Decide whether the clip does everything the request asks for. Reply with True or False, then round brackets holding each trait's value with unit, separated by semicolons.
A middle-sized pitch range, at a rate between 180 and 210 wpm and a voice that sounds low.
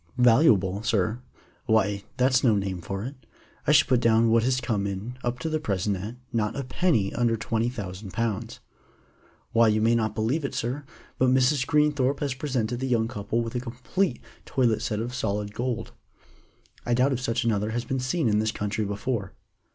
True (3.3 semitones; 190 wpm; 115 Hz)